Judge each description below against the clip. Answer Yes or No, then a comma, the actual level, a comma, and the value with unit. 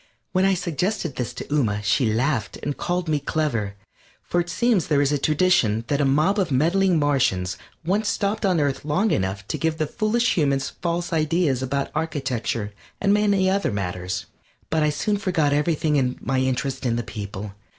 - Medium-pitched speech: Yes, medium, 150 Hz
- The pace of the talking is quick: No, average, 185 wpm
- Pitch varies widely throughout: Yes, wide, 5.8 semitones